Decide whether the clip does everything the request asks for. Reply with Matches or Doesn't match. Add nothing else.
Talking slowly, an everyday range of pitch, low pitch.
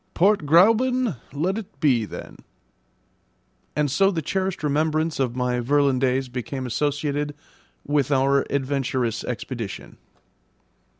Doesn't match